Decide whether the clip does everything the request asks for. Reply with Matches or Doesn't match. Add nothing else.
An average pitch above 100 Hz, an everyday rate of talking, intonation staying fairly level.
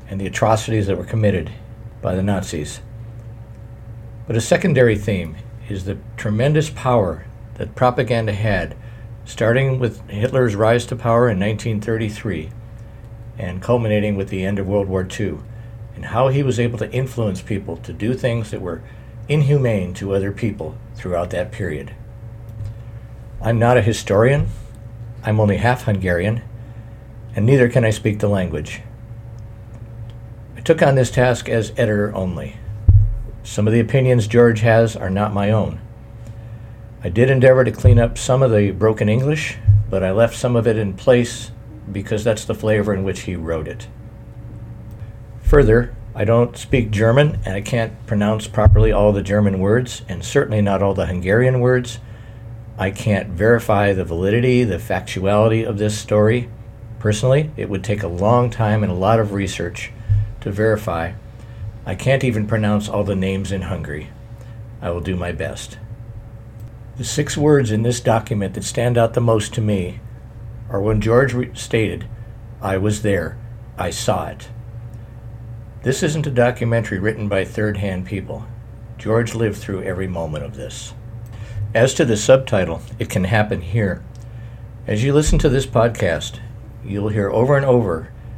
Matches